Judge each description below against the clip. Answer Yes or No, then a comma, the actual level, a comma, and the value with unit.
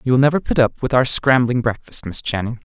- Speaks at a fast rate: Yes, fast, 245 wpm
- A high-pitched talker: No, low, 120 Hz